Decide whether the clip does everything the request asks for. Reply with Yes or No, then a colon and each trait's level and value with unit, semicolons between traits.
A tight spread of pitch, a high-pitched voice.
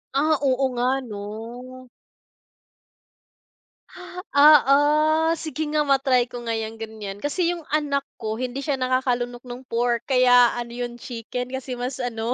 Yes: narrow, 2.2 semitones; very high, 250 Hz